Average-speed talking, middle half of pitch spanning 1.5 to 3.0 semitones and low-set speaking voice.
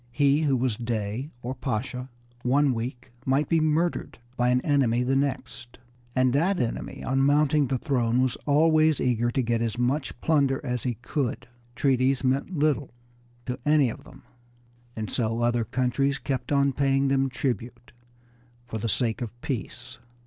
Yes: average, 165 wpm; average, 2.7 semitones; low, 130 Hz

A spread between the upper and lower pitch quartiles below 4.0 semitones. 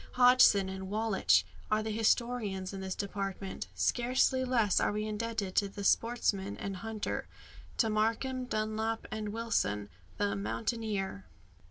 Yes: average, 2.9 semitones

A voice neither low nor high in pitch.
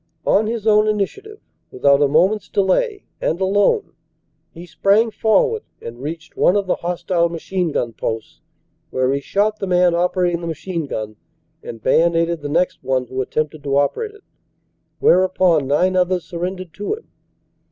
Yes: medium, 180 Hz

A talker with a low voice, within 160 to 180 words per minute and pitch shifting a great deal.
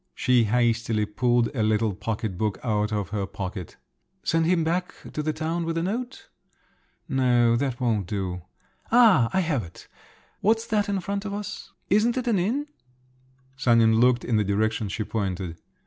Yes: low, 120 Hz; average, 170 wpm; wide, 8.8 semitones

